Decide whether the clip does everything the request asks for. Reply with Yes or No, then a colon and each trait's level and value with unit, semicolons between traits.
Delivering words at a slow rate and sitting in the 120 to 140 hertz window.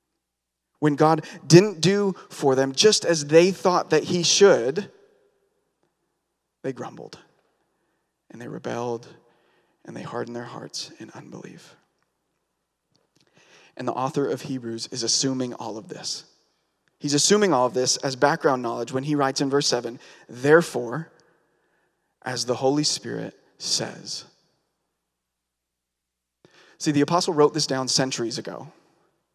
Yes: slow, 130 wpm; low, 135 Hz